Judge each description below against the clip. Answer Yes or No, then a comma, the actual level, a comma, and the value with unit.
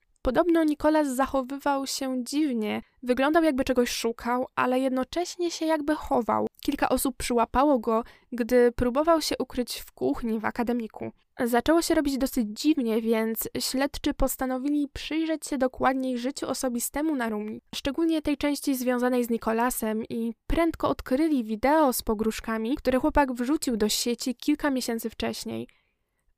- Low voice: No, very high, 260 Hz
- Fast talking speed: No, average, 140 wpm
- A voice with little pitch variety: No, average, 3.9 semitones